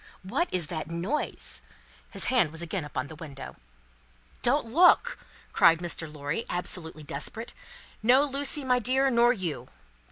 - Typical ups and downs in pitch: No, wide, 8.1 semitones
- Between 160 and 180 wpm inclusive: No, average, 140 wpm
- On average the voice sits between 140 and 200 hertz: Yes, medium, 185 Hz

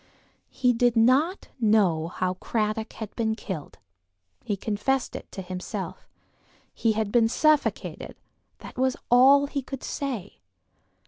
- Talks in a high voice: Yes, high, 225 Hz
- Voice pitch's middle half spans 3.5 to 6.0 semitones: Yes, average, 4.1 semitones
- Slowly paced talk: Yes, slow, 130 wpm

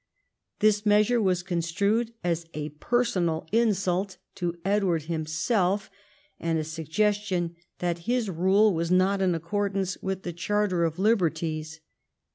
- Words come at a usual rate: No, slow, 130 wpm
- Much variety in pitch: No, average, 3.6 semitones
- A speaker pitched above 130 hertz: Yes, medium, 185 Hz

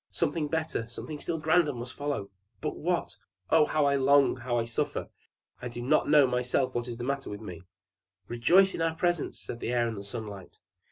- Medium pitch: No, low, 130 Hz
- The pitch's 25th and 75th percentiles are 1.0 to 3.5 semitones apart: No, average, 4.6 semitones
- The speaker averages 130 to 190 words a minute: No, fast, 205 wpm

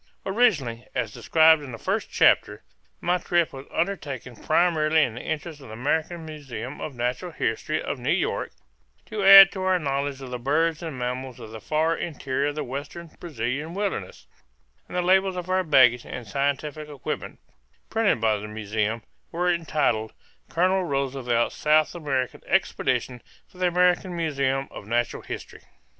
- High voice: No, medium, 145 Hz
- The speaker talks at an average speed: Yes, average, 165 wpm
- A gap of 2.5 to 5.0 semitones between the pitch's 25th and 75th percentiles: No, wide, 5.4 semitones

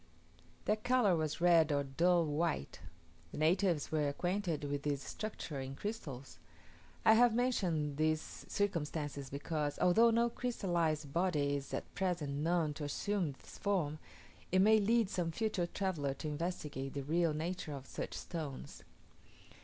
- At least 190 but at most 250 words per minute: No, average, 145 wpm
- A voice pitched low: No, medium, 165 Hz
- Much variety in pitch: No, average, 4.6 semitones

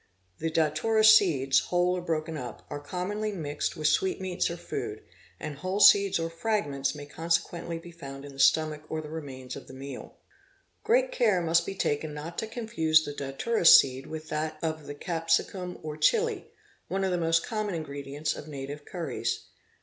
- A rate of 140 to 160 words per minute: No, average, 175 wpm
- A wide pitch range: No, average, 4.0 semitones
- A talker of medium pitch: Yes, medium, 160 Hz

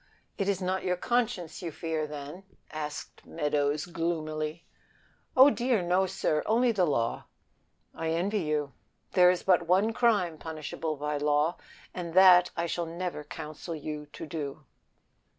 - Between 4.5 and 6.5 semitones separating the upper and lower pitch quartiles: No, average, 3.3 semitones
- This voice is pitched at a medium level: Yes, medium, 165 Hz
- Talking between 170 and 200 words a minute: No, average, 150 wpm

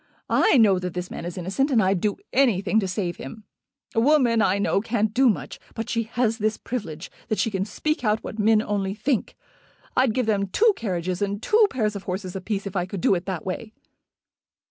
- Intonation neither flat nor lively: Yes, average, 3.4 semitones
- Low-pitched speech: No, high, 210 Hz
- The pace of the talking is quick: Yes, fast, 220 wpm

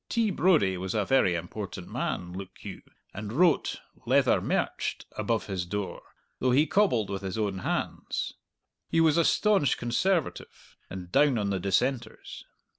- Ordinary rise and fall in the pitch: No, wide, 7.7 semitones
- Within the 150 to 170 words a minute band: Yes, average, 155 wpm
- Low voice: Yes, low, 110 Hz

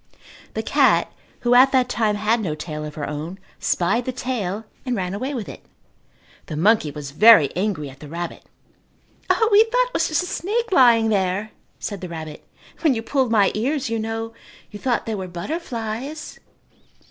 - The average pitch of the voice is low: No, high, 220 Hz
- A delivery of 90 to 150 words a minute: No, average, 185 wpm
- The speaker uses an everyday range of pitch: No, wide, 6.1 semitones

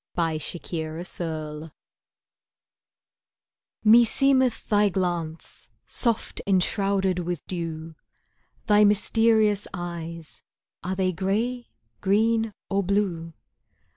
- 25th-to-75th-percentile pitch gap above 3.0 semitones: Yes, average, 3.9 semitones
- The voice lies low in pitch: No, high, 190 Hz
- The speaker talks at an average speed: No, slow, 75 wpm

